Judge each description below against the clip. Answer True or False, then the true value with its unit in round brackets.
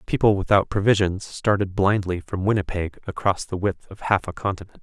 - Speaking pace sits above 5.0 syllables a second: True (5.5 syllables/s)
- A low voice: True (95 Hz)